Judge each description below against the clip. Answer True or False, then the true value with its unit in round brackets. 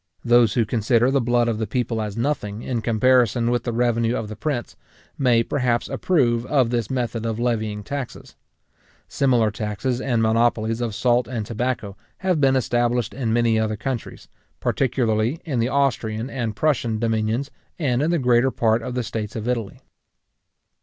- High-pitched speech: False (120 Hz)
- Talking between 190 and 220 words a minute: False (170 wpm)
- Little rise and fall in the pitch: True (2.3 semitones)